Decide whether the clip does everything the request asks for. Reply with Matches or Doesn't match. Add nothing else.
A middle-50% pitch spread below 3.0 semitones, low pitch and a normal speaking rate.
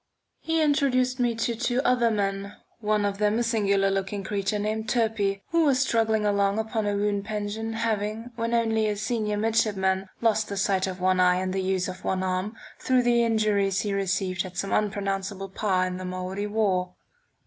Doesn't match